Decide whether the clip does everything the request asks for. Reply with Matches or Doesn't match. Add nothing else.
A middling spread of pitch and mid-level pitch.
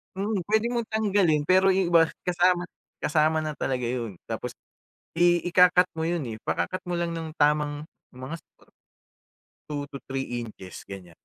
Matches